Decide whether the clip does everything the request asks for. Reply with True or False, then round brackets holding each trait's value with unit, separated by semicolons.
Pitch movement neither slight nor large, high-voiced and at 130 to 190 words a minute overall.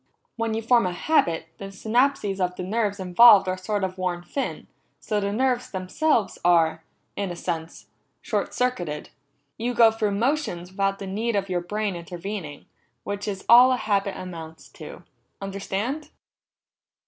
True (3.9 semitones; 200 Hz; 160 wpm)